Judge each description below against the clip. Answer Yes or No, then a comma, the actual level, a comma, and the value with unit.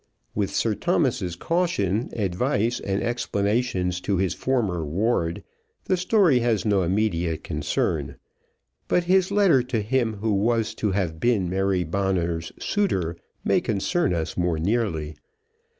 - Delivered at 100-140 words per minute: Yes, slow, 135 wpm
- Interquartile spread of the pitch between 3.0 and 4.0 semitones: No, wide, 5.4 semitones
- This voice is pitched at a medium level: No, low, 100 Hz